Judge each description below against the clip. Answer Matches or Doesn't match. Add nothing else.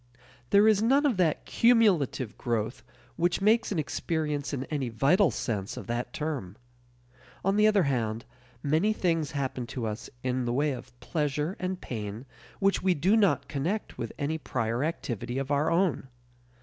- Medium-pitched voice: Matches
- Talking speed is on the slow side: Doesn't match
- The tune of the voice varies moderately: Doesn't match